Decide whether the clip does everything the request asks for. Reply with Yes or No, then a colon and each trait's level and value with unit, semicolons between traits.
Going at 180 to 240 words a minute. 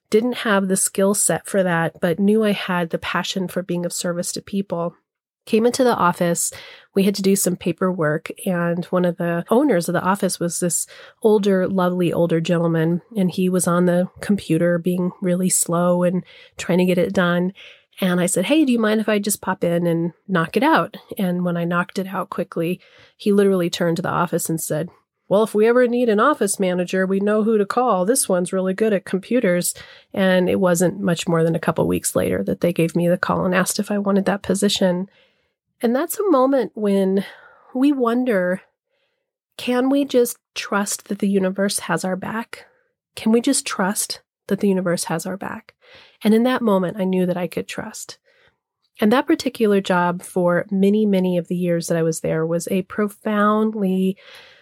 Yes: fast, 205 wpm